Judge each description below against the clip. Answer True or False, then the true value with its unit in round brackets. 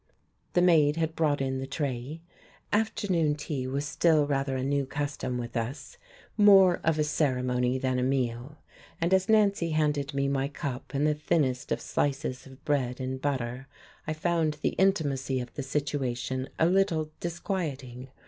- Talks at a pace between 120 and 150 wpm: False (165 wpm)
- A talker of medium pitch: True (145 Hz)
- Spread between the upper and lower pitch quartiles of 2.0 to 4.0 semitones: True (3.5 semitones)